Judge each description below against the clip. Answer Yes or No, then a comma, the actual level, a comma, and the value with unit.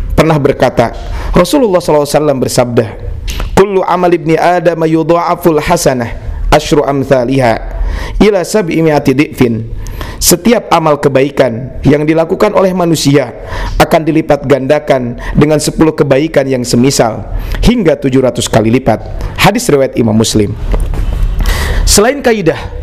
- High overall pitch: No, medium, 140 Hz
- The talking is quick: No, average, 110 wpm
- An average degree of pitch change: No, wide, 6.3 semitones